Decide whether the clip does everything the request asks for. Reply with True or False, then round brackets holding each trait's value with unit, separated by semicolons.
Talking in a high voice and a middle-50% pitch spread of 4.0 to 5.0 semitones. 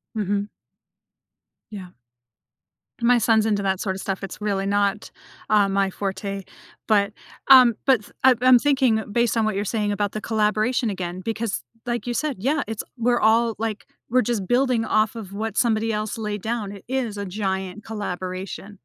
False (215 Hz; 2.8 semitones)